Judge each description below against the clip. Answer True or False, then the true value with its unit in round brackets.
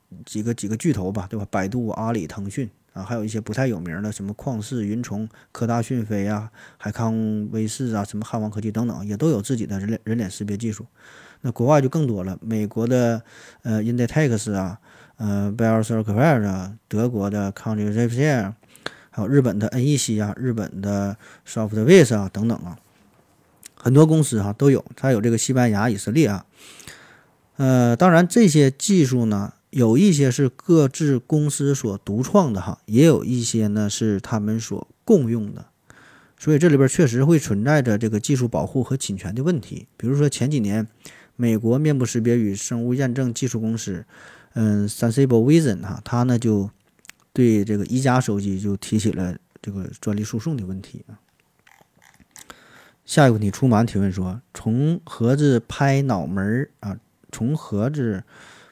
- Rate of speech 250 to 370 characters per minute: True (290 characters per minute)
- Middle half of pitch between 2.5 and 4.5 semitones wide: True (3.9 semitones)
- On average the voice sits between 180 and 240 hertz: False (115 Hz)